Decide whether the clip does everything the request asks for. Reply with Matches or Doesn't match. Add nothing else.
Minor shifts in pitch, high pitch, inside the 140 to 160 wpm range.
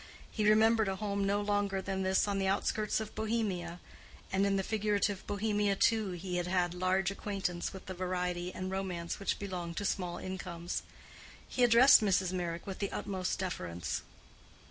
Doesn't match